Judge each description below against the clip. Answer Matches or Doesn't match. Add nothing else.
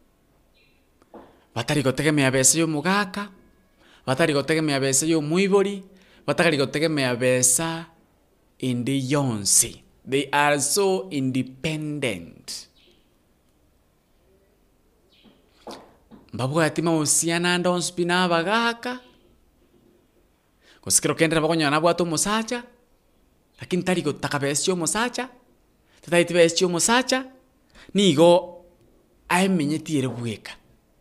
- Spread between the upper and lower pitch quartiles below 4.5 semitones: Doesn't match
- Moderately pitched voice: Matches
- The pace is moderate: Doesn't match